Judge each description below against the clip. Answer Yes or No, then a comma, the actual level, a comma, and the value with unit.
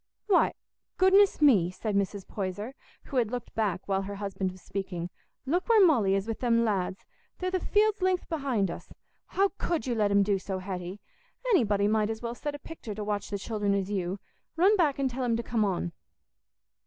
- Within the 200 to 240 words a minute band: Yes, fast, 205 wpm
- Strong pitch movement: Yes, wide, 6.2 semitones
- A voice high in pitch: Yes, high, 215 Hz